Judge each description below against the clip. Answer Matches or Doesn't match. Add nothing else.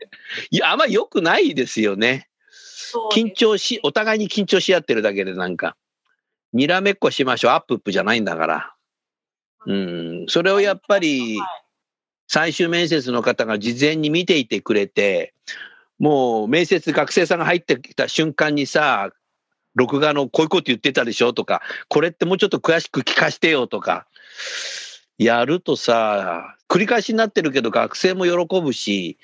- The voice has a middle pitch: Matches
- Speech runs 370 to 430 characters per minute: Doesn't match